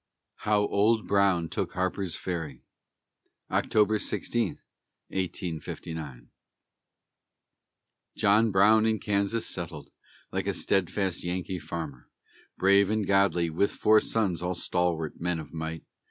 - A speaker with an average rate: No, slow, 110 wpm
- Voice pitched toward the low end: Yes, very low, 95 Hz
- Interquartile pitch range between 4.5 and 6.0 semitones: No, average, 3.4 semitones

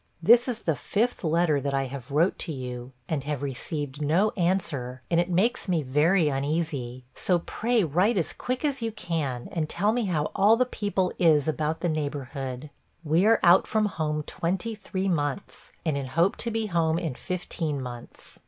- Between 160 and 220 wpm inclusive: Yes, average, 190 wpm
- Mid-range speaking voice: Yes, medium, 165 Hz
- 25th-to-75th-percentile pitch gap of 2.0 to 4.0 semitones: No, average, 5.2 semitones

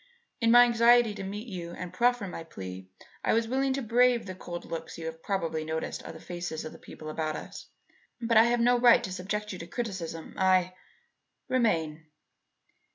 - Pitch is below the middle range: No, high, 190 Hz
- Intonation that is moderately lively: No, wide, 6.2 semitones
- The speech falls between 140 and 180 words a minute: No, average, 200 wpm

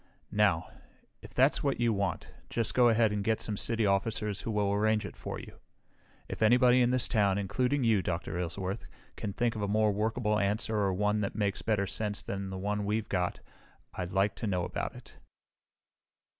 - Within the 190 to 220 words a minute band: Yes, average, 195 wpm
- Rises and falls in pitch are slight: Yes, narrow, 2.3 semitones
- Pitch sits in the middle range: No, low, 105 Hz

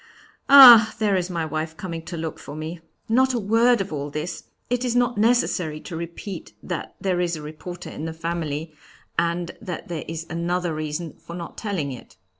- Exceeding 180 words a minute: Yes, average, 190 wpm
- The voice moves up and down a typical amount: Yes, average, 4.4 semitones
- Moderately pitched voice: Yes, medium, 170 Hz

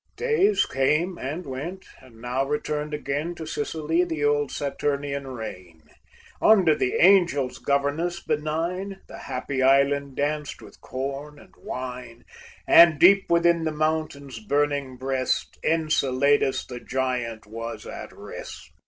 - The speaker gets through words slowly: Yes, slow, 125 wpm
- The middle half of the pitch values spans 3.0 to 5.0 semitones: Yes, average, 3.6 semitones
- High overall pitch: No, medium, 145 Hz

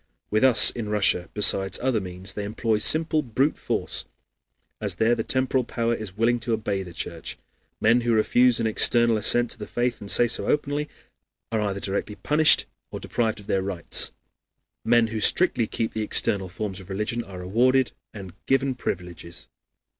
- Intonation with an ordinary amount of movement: Yes, average, 3.5 semitones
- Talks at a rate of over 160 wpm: Yes, average, 175 wpm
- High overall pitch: No, low, 110 Hz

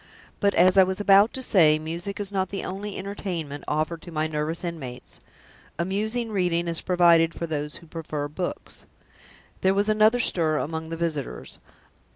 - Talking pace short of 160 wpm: No, average, 170 wpm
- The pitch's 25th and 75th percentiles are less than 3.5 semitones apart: No, average, 3.8 semitones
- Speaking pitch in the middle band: Yes, medium, 170 Hz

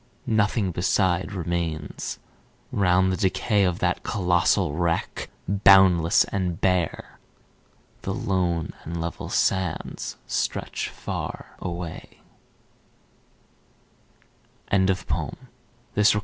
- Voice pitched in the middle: No, very low, 90 Hz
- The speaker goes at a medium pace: No, slow, 90 wpm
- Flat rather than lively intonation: Yes, narrow, 2.2 semitones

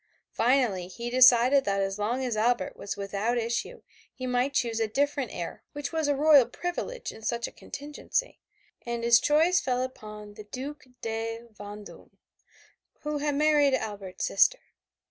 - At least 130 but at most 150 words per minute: No, average, 160 wpm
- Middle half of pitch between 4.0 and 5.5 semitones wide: Yes, average, 4.9 semitones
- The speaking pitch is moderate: No, high, 245 Hz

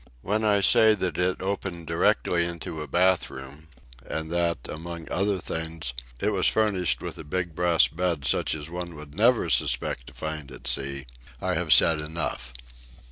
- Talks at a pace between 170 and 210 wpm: Yes, average, 175 wpm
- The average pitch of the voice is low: Yes, very low, 85 Hz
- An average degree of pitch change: Yes, average, 3.1 semitones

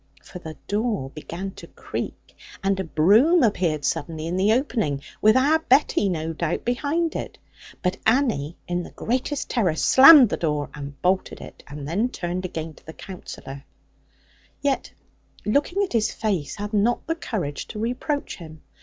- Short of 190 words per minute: Yes, average, 165 wpm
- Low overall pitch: No, high, 195 Hz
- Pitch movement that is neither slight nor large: No, wide, 7.5 semitones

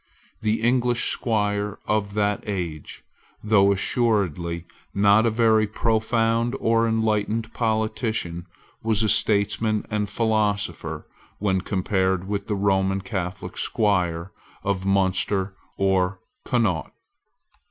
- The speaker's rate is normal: No, slow, 110 wpm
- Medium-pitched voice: No, low, 105 Hz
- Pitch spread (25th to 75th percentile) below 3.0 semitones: Yes, narrow, 2.5 semitones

